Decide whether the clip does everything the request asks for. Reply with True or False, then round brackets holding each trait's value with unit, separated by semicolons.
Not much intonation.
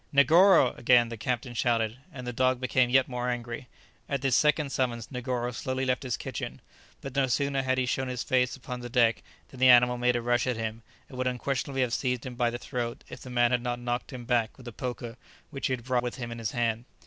True (1.3 semitones)